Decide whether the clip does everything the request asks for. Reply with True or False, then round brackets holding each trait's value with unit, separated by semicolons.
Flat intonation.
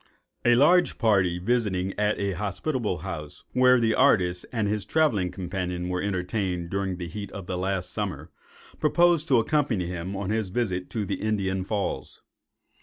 False (4.1 semitones)